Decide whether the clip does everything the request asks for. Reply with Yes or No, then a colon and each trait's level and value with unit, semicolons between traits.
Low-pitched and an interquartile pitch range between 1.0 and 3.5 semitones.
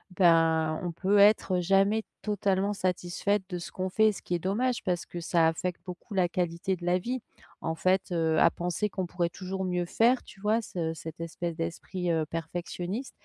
No: medium, 180 Hz; narrow, 2.6 semitones